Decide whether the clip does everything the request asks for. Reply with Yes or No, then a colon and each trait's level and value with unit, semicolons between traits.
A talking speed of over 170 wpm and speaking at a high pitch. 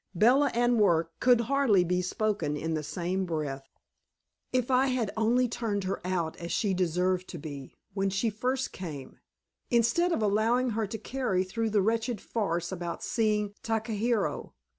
No: average, 160 wpm; high, 210 Hz